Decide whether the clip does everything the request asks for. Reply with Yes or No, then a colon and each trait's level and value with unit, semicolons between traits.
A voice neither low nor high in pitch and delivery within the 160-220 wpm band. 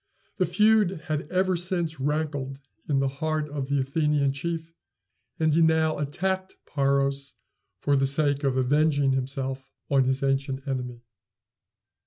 No: medium, 145 Hz; average, 140 wpm